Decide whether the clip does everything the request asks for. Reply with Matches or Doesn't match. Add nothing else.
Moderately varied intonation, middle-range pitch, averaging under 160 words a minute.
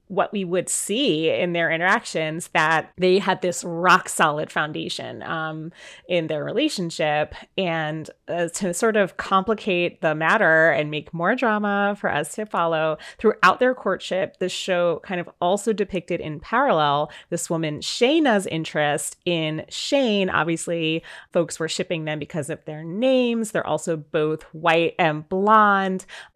Matches